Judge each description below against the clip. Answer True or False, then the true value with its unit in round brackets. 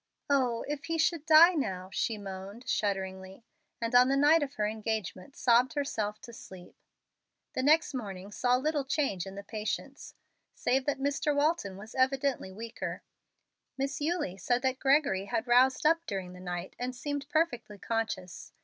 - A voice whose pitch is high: True (245 Hz)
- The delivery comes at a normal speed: True (165 wpm)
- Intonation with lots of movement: True (6.0 semitones)